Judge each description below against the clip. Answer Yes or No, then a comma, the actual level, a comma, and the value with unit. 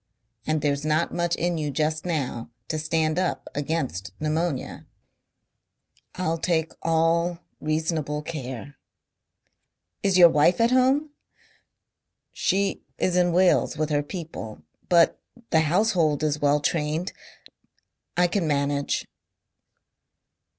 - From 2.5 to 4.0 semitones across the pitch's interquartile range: Yes, average, 2.8 semitones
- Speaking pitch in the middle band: Yes, medium, 160 Hz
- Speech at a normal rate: No, slow, 115 wpm